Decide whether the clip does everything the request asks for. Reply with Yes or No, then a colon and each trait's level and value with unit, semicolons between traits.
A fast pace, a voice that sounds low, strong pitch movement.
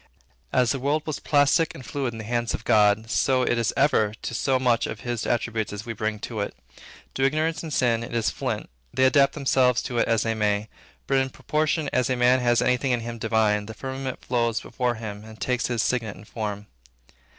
No: fast, 225 wpm; low, 120 Hz; average, 3.1 semitones